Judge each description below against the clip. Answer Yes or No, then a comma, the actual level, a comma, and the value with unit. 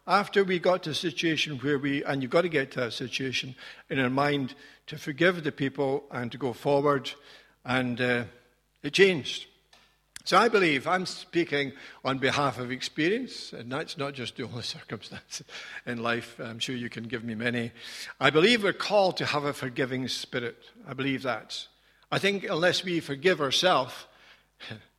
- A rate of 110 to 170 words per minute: No, average, 180 wpm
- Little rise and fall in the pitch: No, average, 4.0 semitones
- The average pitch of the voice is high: No, medium, 140 Hz